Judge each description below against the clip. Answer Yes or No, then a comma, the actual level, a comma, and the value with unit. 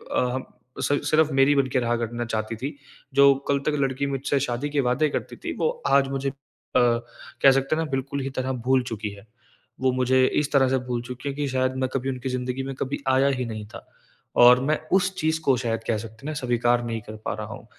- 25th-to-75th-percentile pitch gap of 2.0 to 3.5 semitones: Yes, narrow, 2.5 semitones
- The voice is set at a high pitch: No, low, 130 Hz